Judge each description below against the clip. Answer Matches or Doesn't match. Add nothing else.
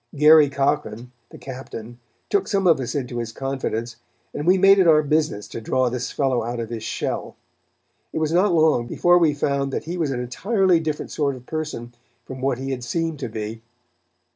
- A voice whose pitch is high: Doesn't match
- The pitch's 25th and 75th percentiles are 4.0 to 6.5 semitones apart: Matches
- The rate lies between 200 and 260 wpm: Matches